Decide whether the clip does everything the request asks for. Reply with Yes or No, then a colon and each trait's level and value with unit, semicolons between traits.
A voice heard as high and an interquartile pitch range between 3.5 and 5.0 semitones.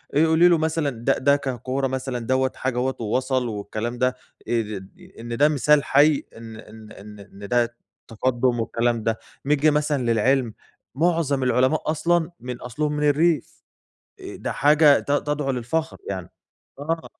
No: low, 130 Hz; average, 4.0 semitones